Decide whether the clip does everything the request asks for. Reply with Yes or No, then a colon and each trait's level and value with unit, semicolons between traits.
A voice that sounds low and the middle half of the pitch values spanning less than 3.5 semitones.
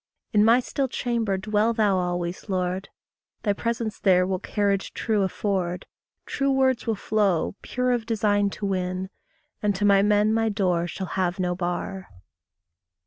No: high, 200 Hz; average, 3.1 semitones